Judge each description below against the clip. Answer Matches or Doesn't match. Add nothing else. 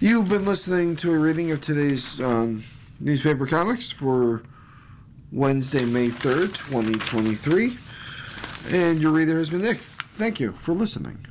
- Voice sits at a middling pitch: Matches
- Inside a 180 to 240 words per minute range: Doesn't match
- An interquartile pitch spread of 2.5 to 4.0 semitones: Doesn't match